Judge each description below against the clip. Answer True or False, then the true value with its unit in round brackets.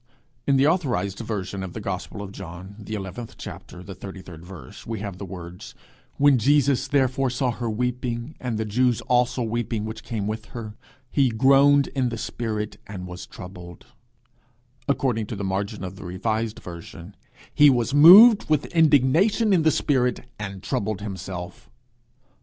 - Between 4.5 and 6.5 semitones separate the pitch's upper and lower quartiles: True (5.3 semitones)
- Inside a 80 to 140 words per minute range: False (165 wpm)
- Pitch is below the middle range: True (110 Hz)